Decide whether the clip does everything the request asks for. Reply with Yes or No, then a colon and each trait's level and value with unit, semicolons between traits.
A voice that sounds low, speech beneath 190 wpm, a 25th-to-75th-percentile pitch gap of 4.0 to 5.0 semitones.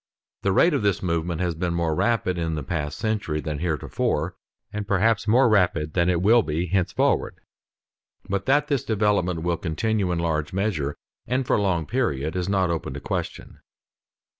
Yes: very low, 90 Hz; average, 180 wpm; average, 4.5 semitones